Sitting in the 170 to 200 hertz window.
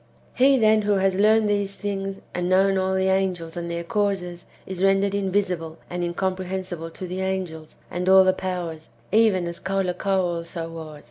Yes: high, 190 Hz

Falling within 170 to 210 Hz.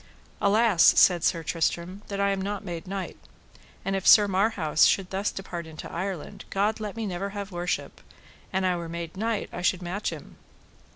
Yes: high, 190 Hz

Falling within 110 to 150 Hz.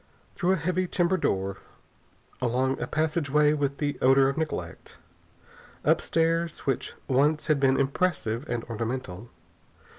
Yes: medium, 140 Hz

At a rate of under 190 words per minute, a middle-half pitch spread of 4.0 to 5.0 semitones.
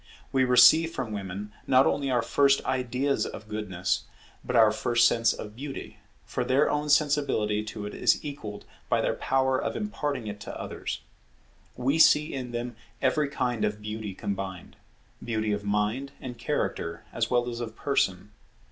Yes: average, 165 wpm; average, 4.5 semitones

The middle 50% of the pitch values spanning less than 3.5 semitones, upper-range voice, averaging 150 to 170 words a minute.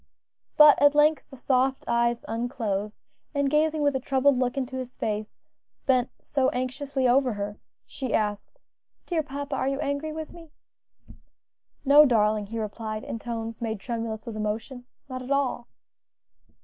No: average, 3.9 semitones; very high, 255 Hz; average, 155 wpm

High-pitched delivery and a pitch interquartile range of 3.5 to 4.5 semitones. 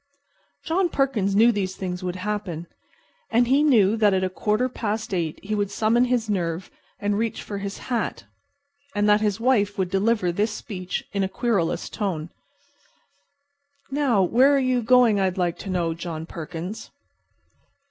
Yes: high, 205 Hz; average, 3.9 semitones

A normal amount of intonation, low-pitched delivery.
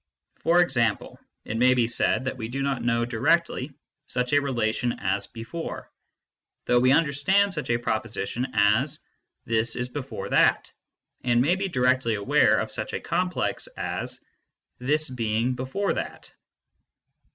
Yes: average, 3.7 semitones; low, 125 Hz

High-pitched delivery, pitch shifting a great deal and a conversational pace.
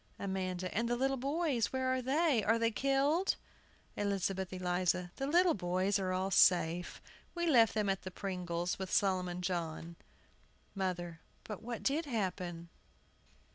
Yes: high, 195 Hz; wide, 6.0 semitones; average, 145 wpm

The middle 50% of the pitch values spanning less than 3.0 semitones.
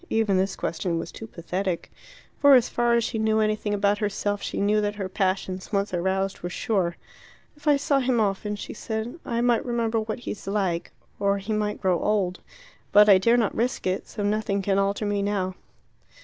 Yes: narrow, 2.5 semitones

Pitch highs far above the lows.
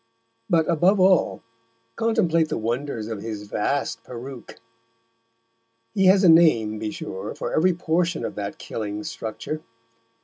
Yes: wide, 7.9 semitones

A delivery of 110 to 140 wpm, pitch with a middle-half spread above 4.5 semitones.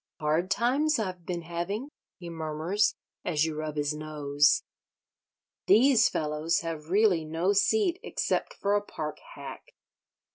Yes: slow, 135 wpm; average, 5.0 semitones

